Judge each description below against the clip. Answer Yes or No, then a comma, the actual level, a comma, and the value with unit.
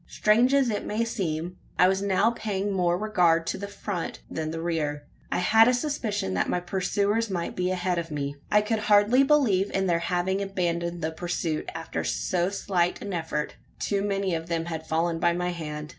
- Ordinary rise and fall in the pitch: Yes, average, 3.4 semitones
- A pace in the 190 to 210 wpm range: Yes, average, 200 wpm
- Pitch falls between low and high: Yes, medium, 180 Hz